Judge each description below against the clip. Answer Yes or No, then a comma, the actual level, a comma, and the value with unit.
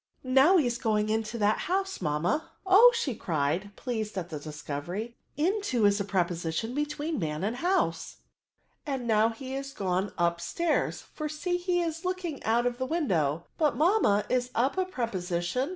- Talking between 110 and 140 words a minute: No, average, 170 wpm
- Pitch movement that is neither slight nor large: No, wide, 8.6 semitones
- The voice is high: Yes, high, 235 Hz